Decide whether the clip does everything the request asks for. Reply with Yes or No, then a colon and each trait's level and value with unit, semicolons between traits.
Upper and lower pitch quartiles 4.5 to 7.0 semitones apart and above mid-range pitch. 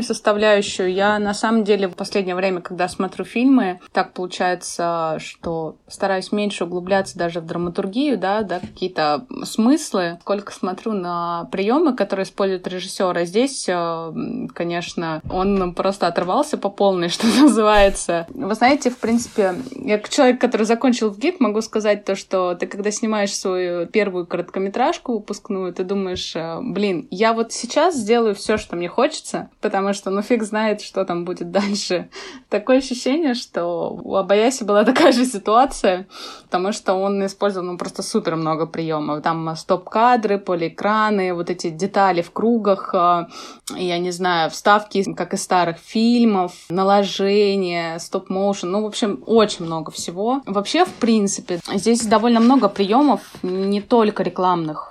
No: average, 3.5 semitones; high, 200 Hz